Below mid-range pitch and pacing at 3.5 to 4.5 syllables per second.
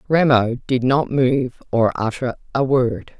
Yes: low, 125 Hz; 3.7 syllables/s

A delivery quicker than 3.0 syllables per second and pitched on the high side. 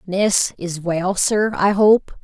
No: 2.9 syllables/s; high, 195 Hz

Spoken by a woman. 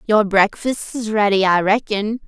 Yes: female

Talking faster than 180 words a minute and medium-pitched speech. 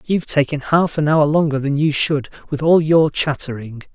Yes: average, 200 wpm; medium, 150 Hz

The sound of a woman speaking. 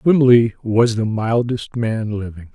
No: male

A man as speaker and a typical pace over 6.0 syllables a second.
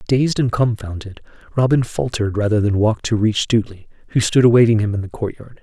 Yes: male; 6.2 syllables/s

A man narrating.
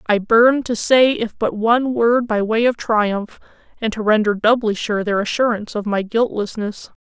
No: female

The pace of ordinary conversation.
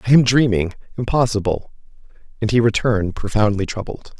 No: slow, 130 wpm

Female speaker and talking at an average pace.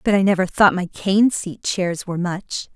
No: female; fast, 220 wpm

